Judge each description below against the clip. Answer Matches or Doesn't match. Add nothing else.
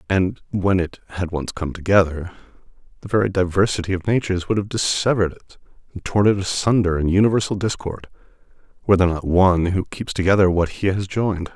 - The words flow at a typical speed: Matches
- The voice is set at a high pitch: Doesn't match